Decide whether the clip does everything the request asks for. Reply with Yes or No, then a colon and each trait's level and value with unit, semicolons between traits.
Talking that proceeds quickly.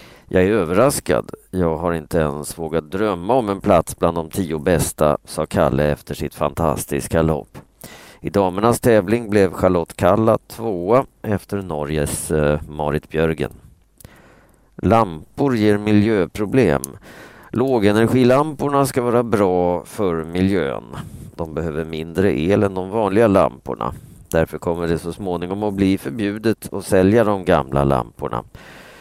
No: average, 130 wpm